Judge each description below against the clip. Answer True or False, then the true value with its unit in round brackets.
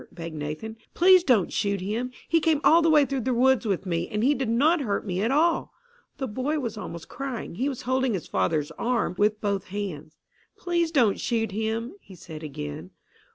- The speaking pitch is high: True (225 Hz)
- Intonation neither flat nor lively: False (6.3 semitones)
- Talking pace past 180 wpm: True (200 wpm)